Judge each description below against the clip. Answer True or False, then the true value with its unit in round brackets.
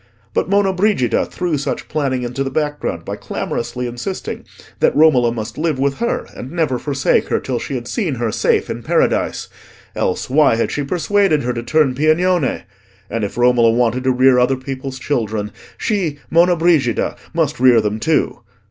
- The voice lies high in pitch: False (130 Hz)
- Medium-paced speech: True (170 wpm)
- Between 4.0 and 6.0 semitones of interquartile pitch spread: True (4.7 semitones)